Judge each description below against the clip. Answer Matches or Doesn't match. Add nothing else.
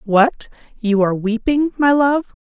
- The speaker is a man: Doesn't match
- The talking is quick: Doesn't match